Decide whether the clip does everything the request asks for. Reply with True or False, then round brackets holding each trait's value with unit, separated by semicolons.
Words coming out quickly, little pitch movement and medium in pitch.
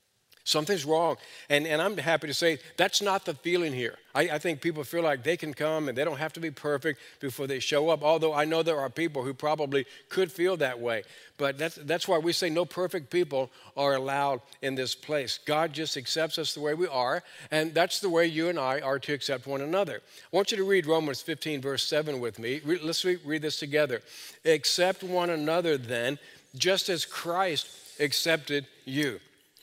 False (210 wpm; 3.3 semitones; 155 Hz)